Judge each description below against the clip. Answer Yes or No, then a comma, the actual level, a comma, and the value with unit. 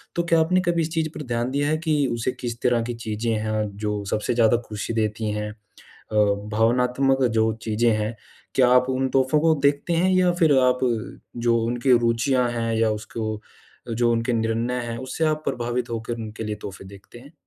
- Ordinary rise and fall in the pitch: Yes, average, 3.0 semitones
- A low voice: Yes, low, 120 Hz